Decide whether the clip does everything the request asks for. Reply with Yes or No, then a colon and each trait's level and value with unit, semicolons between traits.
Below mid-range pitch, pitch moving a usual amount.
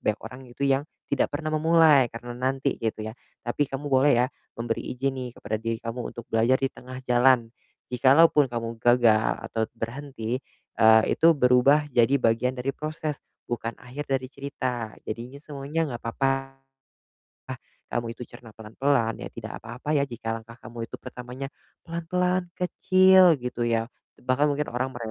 Yes: low, 125 Hz; average, 3.3 semitones